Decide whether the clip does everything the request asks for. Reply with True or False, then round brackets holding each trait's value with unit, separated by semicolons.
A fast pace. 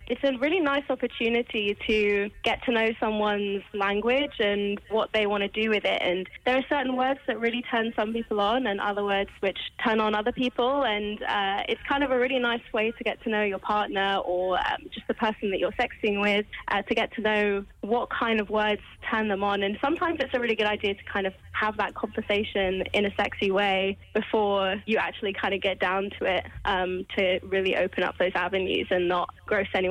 True (225 wpm)